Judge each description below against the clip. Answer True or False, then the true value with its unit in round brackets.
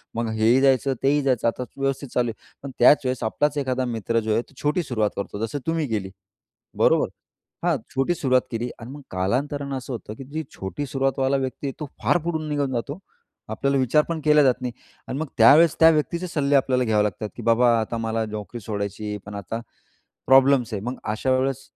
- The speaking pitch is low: True (130 Hz)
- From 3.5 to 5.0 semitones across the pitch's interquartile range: True (3.9 semitones)